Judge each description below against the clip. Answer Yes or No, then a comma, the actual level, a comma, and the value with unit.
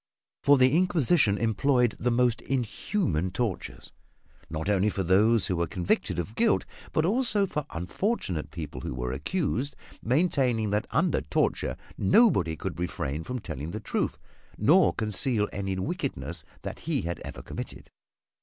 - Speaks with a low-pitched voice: Yes, low, 110 Hz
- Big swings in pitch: Yes, wide, 8.2 semitones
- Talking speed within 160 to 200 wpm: No, average, 145 wpm